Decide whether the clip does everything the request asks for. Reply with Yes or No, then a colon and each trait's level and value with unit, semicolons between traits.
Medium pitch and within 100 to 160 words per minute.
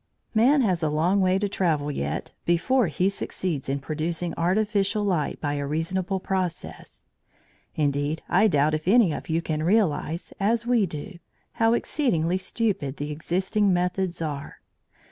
Yes: medium, 175 Hz; average, 150 wpm